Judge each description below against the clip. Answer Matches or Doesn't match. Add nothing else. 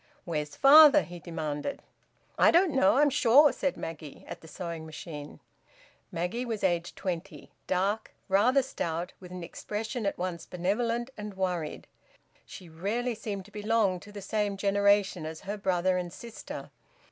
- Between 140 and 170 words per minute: Matches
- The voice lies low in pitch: Doesn't match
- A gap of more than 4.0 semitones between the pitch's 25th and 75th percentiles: Matches